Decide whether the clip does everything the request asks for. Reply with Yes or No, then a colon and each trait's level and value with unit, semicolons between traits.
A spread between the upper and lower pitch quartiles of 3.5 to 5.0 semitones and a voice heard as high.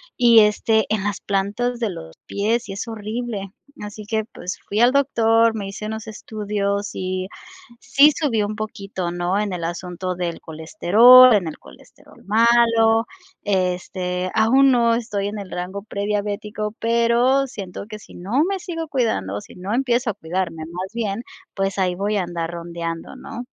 Yes: average, 3.8 semitones; high, 210 Hz